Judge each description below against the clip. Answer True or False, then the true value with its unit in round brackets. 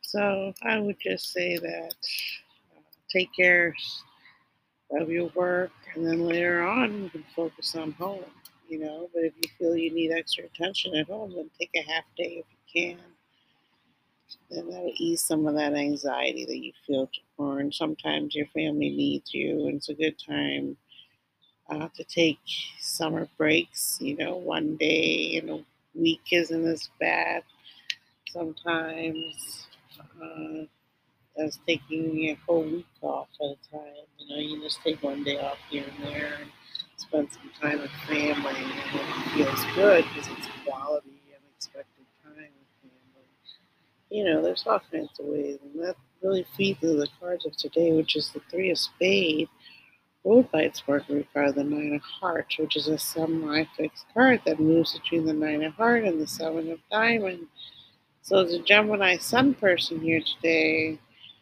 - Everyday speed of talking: True (170 wpm)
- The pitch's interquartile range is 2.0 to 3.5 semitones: True (2.9 semitones)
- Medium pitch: True (160 Hz)